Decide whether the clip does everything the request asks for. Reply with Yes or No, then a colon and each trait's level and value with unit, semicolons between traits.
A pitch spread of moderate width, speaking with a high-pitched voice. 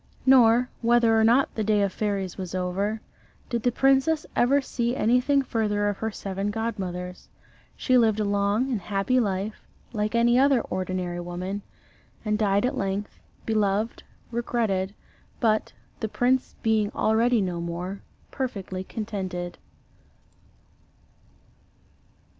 Yes: average, 3.5 semitones; high, 215 Hz